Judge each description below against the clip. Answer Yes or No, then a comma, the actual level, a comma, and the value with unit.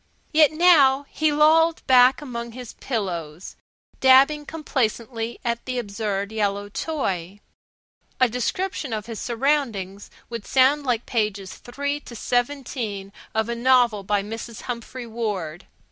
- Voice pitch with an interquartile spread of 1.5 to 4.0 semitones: No, average, 4.5 semitones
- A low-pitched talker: No, high, 235 Hz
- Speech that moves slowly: Yes, slow, 130 wpm